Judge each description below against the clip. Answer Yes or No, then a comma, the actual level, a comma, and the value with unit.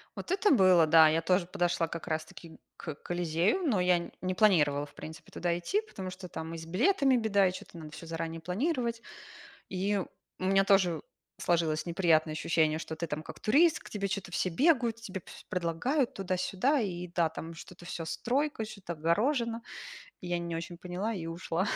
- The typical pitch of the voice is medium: Yes, medium, 180 Hz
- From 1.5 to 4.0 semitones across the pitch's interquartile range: No, average, 4.4 semitones